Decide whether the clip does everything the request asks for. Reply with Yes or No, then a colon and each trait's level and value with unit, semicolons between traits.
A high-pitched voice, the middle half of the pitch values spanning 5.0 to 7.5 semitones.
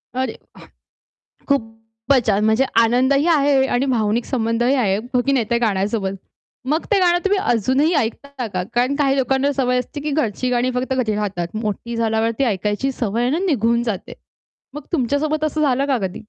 No: very high, 250 Hz; average, 3.7 semitones